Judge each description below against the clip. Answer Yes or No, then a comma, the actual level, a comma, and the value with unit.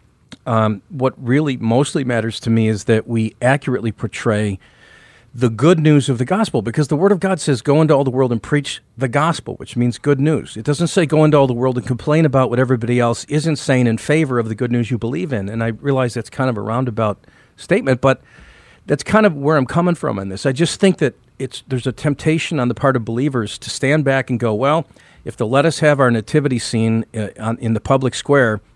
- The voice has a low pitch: Yes, low, 130 Hz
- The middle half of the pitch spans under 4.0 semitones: No, average, 4.3 semitones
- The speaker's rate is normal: No, fast, 235 wpm